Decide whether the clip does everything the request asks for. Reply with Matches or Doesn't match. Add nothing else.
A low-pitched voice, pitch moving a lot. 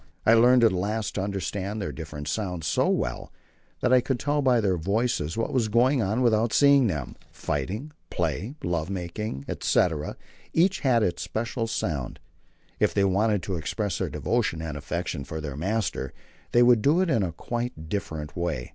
Matches